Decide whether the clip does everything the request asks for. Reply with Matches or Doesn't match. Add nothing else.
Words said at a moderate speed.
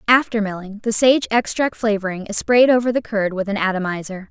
Matches